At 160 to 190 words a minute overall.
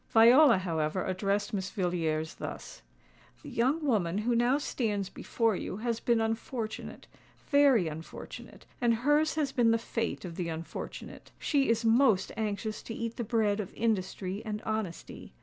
No: average, 150 wpm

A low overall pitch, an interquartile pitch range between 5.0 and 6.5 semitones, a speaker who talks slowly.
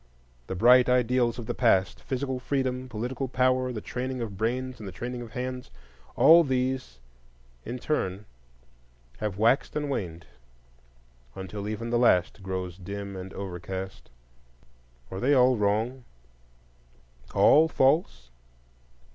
Yes: low, 115 Hz; wide, 5.4 semitones; slow, 120 wpm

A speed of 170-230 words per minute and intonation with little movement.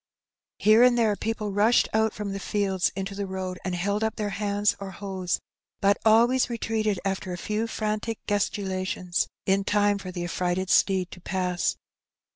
Yes: average, 175 wpm; narrow, 2.3 semitones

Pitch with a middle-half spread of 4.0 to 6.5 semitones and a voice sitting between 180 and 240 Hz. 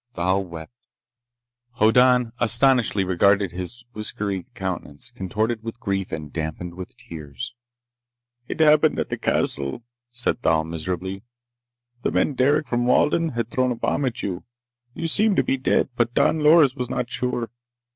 No: wide, 5.6 semitones; low, 115 Hz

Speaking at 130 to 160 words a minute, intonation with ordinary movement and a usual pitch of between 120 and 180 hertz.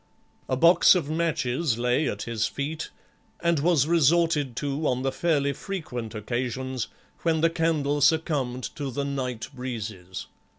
Yes: average, 140 wpm; average, 4.5 semitones; medium, 140 Hz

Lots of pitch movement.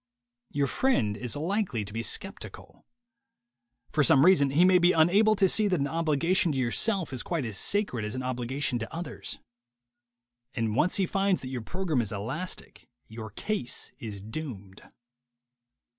Yes: wide, 7.6 semitones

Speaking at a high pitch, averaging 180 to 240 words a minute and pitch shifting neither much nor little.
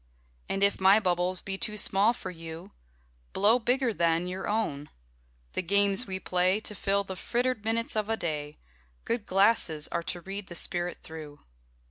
No: high, 195 Hz; average, 170 wpm; average, 3.5 semitones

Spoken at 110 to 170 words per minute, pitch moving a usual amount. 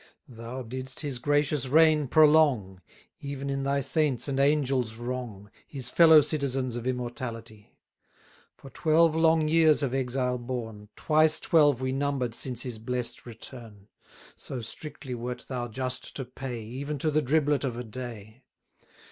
Yes: average, 150 wpm; average, 3.3 semitones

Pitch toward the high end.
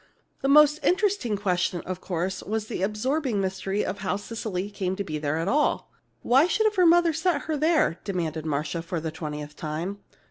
Yes: high, 200 Hz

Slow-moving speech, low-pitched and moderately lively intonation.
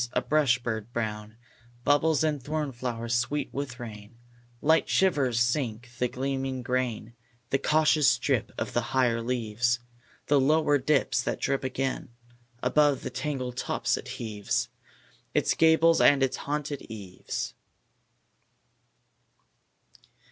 Yes: slow, 120 wpm; low, 130 Hz; average, 3.6 semitones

